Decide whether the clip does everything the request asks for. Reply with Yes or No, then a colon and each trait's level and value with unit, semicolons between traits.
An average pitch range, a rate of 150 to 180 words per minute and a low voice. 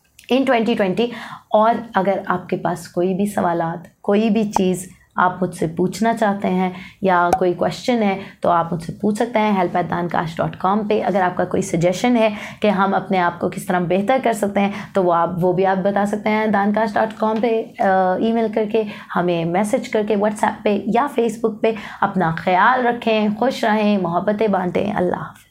No: average, 3.4 semitones; average, 175 wpm; high, 200 Hz